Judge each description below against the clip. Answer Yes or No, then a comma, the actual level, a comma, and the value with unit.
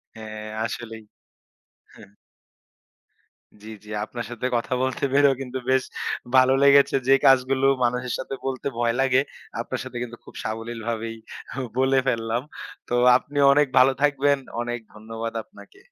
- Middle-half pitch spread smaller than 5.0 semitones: Yes, average, 2.8 semitones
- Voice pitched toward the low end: Yes, low, 125 Hz